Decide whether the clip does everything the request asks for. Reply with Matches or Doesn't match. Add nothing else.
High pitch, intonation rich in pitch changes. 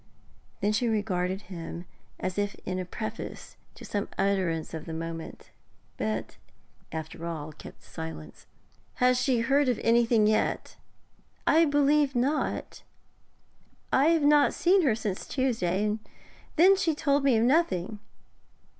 Matches